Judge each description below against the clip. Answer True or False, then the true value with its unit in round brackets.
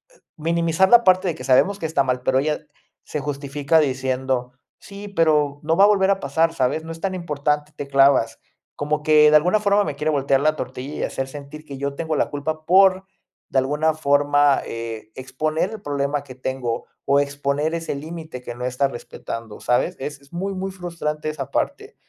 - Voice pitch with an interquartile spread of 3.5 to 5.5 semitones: False (3.1 semitones)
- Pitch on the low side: False (150 Hz)